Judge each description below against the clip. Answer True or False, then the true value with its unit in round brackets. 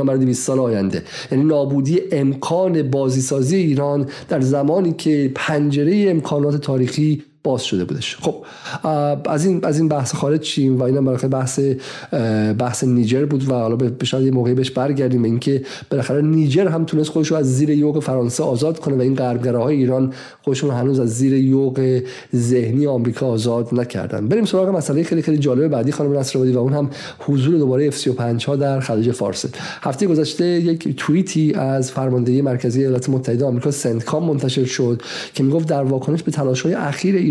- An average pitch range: True (3.0 semitones)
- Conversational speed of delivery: False (170 wpm)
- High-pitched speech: False (135 Hz)